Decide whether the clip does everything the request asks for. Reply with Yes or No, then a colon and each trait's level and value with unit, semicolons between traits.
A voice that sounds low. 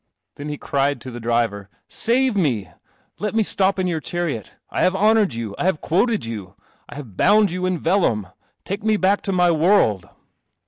No: medium, 175 Hz